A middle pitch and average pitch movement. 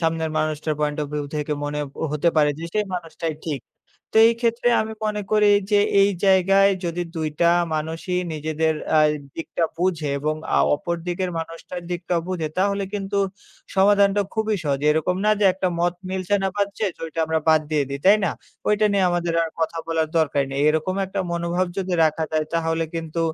Yes: medium, 170 Hz; average, 3.6 semitones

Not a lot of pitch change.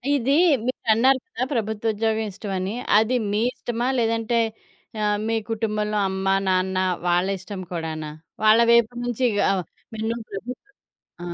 No: average, 3.2 semitones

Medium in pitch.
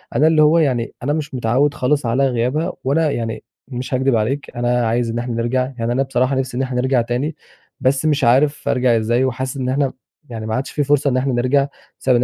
No: low, 130 Hz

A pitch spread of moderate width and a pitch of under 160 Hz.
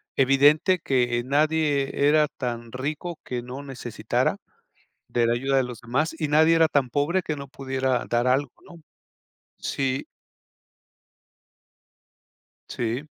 Yes: average, 3.3 semitones; low, 135 Hz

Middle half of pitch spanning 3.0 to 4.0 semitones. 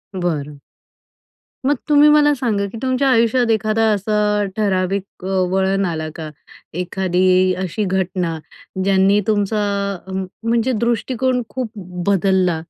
Yes: average, 3.7 semitones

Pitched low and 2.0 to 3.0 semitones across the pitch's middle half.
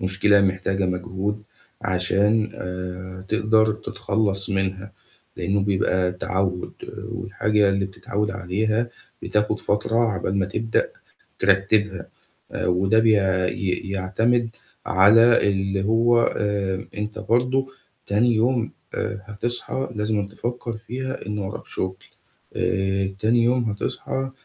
Yes: low, 105 Hz; average, 2.7 semitones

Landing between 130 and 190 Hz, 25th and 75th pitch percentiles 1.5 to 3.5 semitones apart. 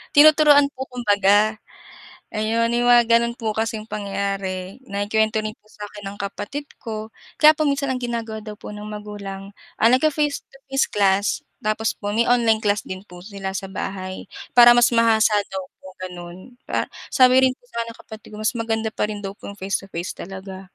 No: high, 215 Hz; average, 3.1 semitones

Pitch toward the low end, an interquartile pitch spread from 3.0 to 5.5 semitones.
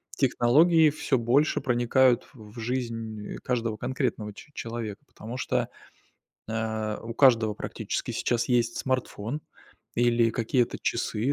No: low, 120 Hz; narrow, 2.5 semitones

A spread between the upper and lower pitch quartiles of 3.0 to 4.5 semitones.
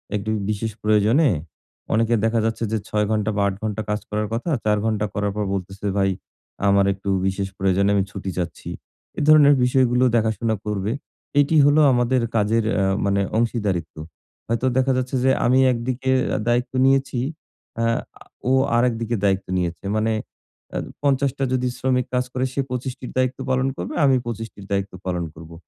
Yes: average, 4.1 semitones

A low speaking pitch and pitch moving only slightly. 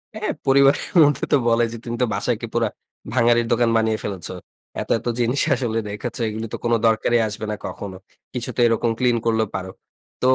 Yes: low, 115 Hz; narrow, 1.6 semitones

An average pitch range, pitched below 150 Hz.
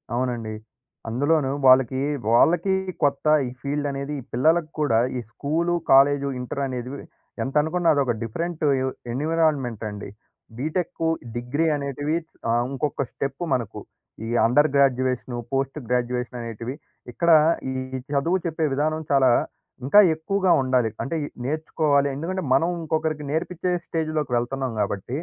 Yes: average, 4.0 semitones; medium, 140 Hz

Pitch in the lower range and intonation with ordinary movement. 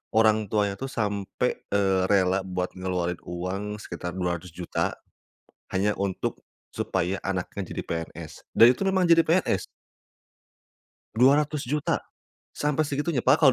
No: low, 100 Hz; wide, 6.3 semitones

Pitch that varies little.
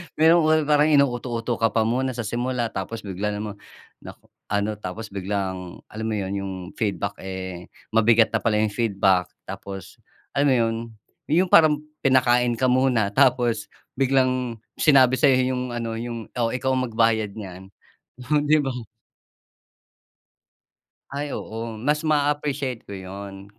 No: average, 4.2 semitones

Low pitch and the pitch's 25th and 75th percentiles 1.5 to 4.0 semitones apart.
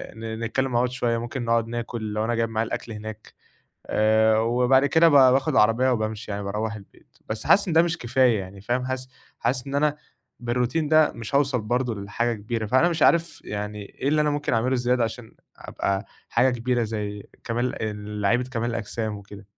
Yes: low, 115 Hz; average, 3.0 semitones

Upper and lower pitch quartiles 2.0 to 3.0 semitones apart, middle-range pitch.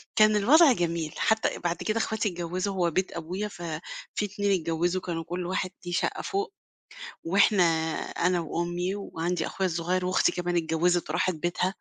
Yes: narrow, 2.6 semitones; medium, 180 Hz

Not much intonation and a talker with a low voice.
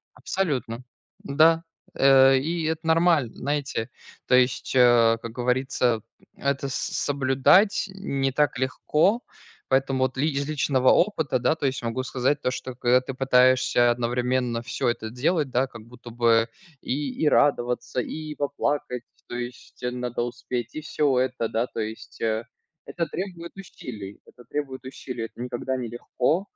No: average, 3.0 semitones; low, 130 Hz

